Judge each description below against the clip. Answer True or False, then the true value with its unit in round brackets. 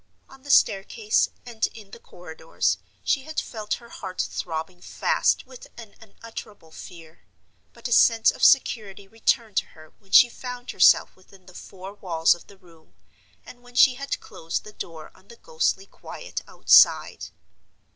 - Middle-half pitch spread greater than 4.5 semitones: True (5.1 semitones)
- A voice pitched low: False (205 Hz)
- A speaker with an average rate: True (165 wpm)